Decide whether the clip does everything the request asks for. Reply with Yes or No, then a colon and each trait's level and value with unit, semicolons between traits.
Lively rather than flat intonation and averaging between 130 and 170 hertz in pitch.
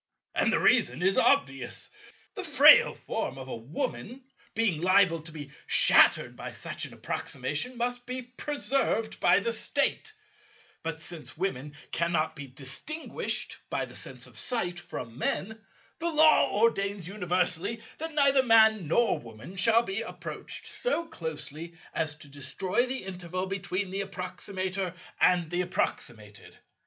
No: wide, 6.6 semitones; medium, 185 Hz